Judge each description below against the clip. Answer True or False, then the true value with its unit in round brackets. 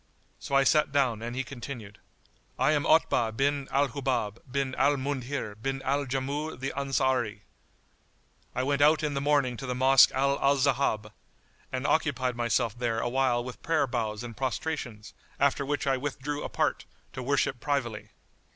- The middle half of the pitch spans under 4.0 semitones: True (2.6 semitones)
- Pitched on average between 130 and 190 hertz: True (135 Hz)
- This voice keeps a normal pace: True (160 wpm)